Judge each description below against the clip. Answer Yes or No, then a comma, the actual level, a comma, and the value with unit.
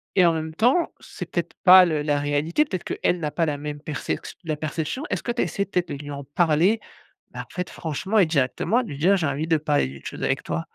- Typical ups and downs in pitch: Yes, average, 4.0 semitones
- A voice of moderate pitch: Yes, medium, 160 Hz